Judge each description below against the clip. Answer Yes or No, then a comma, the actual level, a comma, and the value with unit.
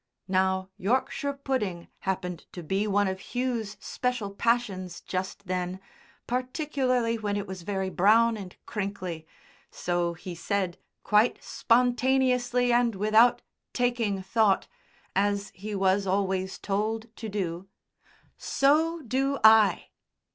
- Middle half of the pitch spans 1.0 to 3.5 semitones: No, average, 4.4 semitones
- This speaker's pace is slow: Yes, slow, 120 wpm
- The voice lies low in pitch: No, high, 205 Hz